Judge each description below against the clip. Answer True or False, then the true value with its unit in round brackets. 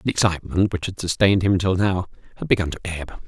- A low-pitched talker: True (95 Hz)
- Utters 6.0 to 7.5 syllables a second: True (6.3 syllables/s)